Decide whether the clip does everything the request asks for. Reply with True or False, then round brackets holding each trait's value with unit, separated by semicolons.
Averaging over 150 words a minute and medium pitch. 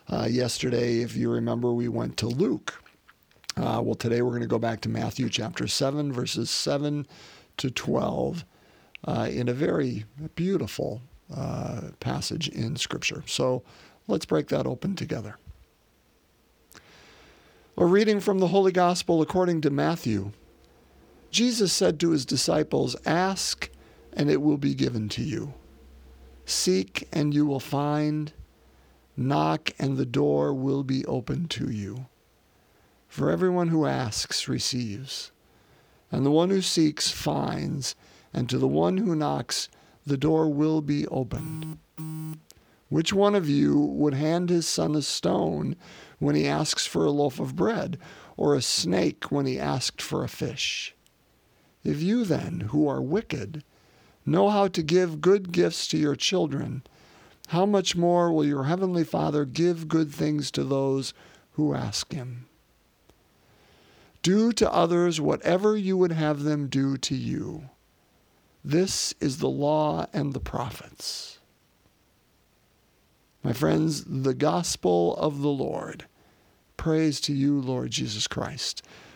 False (140 wpm; 145 Hz)